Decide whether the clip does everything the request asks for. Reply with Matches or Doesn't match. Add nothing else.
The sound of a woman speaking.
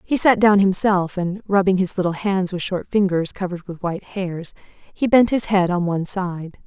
Matches